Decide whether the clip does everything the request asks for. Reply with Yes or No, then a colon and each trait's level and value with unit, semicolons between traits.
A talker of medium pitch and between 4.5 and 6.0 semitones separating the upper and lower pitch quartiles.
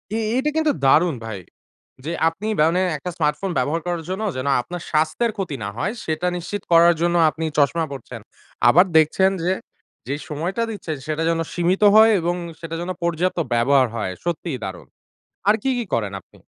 No: medium, 165 Hz; average, 3.5 semitones